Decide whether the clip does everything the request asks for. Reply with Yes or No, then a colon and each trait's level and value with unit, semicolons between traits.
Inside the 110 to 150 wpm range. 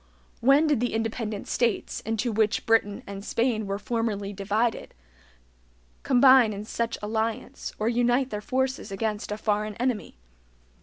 Yes: average, 140 wpm